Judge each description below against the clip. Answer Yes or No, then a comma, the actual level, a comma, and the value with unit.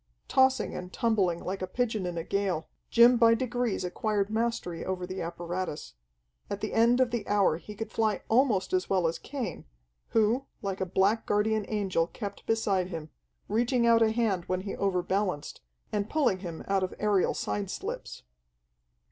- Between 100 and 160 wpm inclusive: No, average, 175 wpm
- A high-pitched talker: Yes, high, 200 Hz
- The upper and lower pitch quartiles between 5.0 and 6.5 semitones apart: No, average, 3.8 semitones